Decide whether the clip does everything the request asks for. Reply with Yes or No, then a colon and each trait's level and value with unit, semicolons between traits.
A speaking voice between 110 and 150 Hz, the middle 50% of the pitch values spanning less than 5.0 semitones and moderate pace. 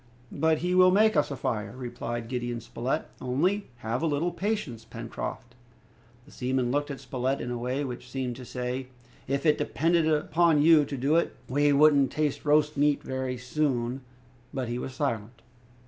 Yes: low, 135 Hz; average, 3.6 semitones; average, 180 wpm